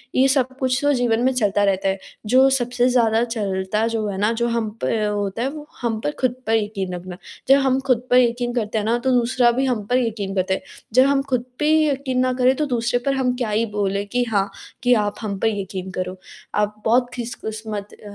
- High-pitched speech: Yes, high, 230 Hz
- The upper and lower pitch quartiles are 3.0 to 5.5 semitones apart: Yes, average, 3.5 semitones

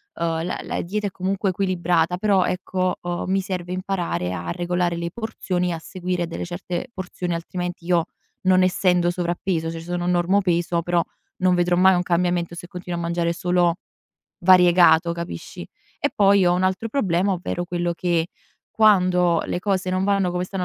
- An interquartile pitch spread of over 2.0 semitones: No, narrow, 1.4 semitones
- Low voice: No, medium, 180 Hz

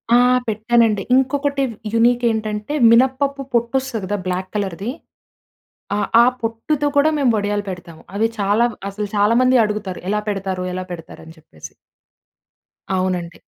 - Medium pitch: No, high, 215 Hz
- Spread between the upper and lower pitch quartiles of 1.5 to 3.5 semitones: No, average, 4.2 semitones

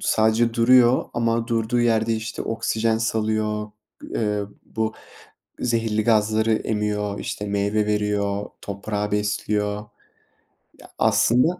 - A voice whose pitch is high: No, low, 110 Hz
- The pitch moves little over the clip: Yes, narrow, 1.7 semitones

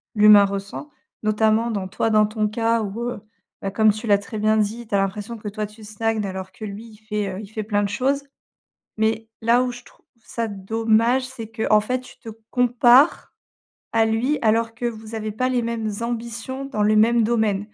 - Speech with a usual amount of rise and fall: No, narrow, 1.8 semitones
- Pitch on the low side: No, high, 220 Hz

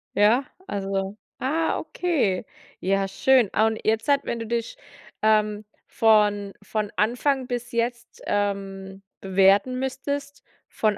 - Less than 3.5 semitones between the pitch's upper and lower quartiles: No, average, 3.8 semitones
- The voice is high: Yes, high, 215 Hz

